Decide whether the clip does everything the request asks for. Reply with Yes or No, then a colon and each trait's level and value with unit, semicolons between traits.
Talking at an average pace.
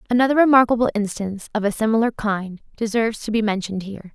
Yes: average, 175 wpm